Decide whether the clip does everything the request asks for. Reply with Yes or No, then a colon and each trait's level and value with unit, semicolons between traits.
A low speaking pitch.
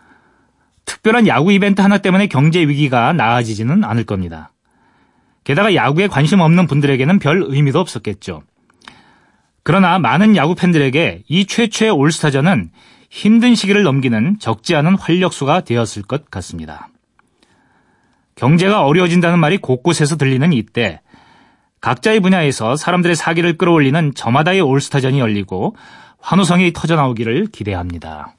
No: medium, 160 Hz